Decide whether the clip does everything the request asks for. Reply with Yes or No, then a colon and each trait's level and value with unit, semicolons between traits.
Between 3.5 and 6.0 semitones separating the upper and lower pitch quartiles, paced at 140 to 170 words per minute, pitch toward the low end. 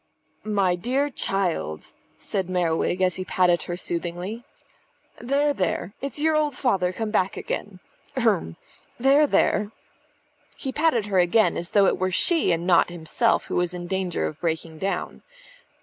No: wide, 5.4 semitones; average, 155 wpm; high, 190 Hz